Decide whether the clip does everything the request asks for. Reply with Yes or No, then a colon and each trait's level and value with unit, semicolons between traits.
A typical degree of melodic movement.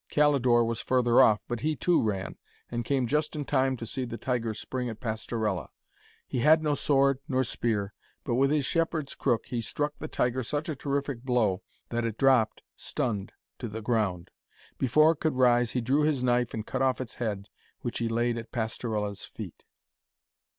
Yes: average, 3.4 semitones